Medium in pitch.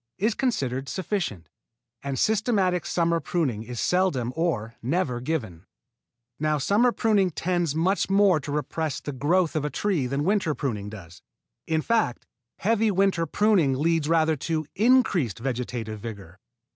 Yes: medium, 160 Hz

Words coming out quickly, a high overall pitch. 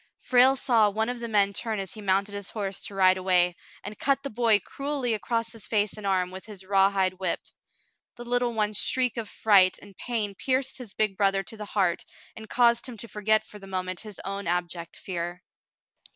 Yes: fast, 210 wpm; high, 205 Hz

